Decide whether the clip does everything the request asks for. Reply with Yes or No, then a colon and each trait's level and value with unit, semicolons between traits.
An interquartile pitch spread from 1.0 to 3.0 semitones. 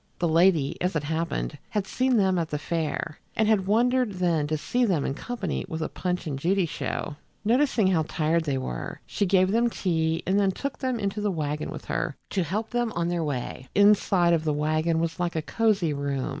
No: average, 4.5 semitones